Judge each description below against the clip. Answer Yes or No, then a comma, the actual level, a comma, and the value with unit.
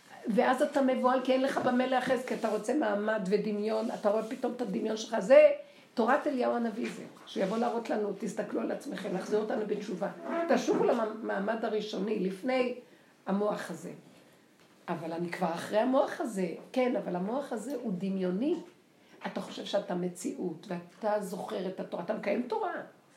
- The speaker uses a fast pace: Yes, fast, 160 wpm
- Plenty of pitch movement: No, average, 4.1 semitones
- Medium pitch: No, high, 220 Hz